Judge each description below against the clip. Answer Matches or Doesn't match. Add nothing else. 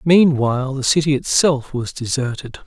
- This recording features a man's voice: Matches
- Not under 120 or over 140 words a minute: Matches